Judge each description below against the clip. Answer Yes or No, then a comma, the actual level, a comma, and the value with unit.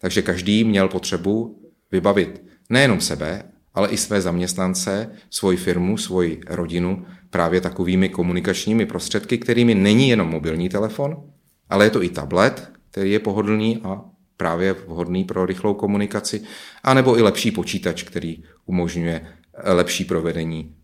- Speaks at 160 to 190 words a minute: No, average, 130 wpm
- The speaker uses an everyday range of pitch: Yes, average, 3.4 semitones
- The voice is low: Yes, very low, 95 Hz